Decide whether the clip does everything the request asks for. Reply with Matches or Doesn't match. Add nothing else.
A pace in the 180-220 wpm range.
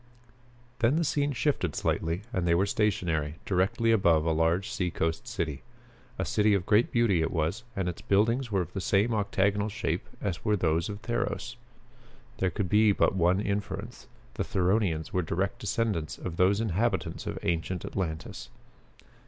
Doesn't match